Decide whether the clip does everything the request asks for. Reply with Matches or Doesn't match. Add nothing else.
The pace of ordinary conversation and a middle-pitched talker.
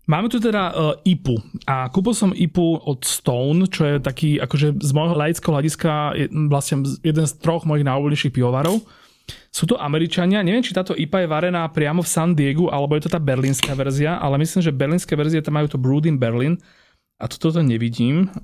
Doesn't match